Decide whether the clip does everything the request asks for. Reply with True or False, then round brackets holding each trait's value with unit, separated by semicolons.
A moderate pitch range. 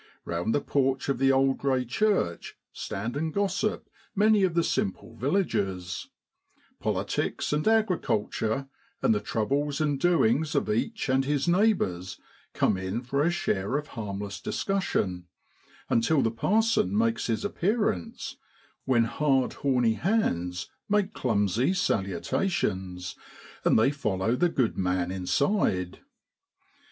False (8.4 semitones)